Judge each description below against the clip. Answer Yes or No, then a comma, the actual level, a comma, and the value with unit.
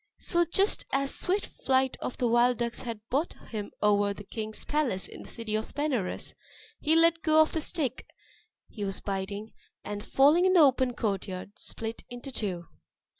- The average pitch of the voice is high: Yes, high, 245 Hz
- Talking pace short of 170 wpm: No, average, 180 wpm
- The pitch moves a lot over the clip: Yes, wide, 6.3 semitones